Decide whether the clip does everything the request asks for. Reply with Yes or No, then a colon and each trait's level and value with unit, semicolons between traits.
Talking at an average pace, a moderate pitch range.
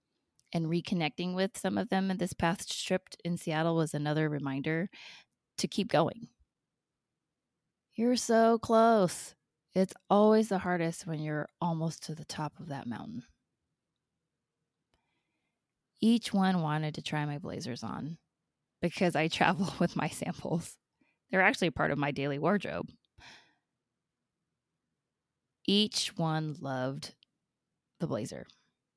No: slow, 125 wpm; average, 3.8 semitones